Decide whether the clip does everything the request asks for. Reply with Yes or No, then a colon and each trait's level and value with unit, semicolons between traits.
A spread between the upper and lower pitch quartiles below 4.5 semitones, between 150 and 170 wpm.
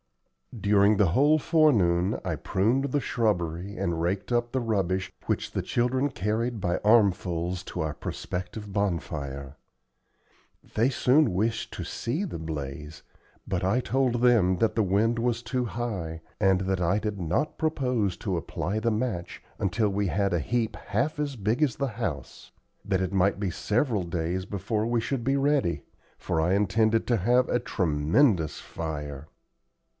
No: average, 5.2 semitones; average, 160 wpm